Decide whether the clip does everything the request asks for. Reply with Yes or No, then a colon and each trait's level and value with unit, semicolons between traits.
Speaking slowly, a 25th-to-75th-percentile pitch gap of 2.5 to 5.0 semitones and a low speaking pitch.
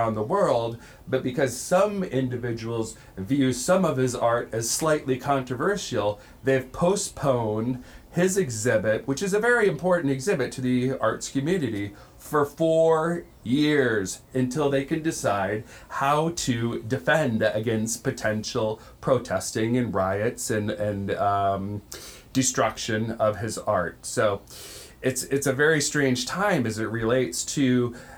Yes: slow, 130 wpm; average, 4.3 semitones; low, 130 Hz